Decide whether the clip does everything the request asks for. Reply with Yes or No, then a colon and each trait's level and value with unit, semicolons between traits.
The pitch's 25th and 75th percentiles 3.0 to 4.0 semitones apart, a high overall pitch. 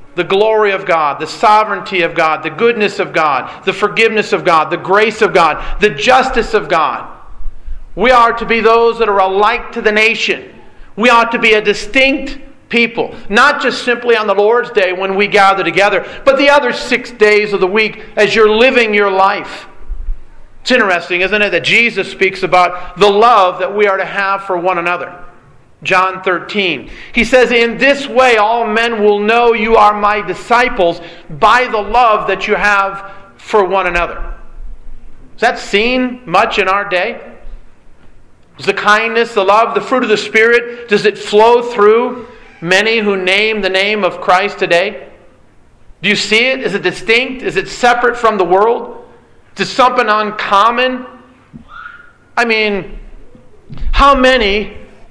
Yes: average, 3.6 semitones; high, 210 Hz